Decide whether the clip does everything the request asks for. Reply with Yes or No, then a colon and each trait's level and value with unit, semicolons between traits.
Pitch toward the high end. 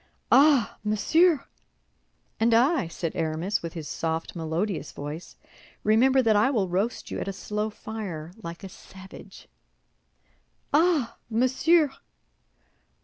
Yes: high, 210 Hz